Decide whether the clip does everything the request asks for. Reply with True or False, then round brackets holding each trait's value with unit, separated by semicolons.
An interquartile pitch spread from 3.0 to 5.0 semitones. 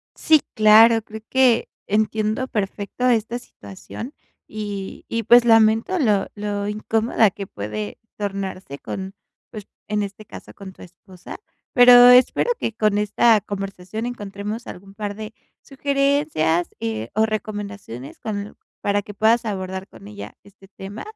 False (2.5 semitones)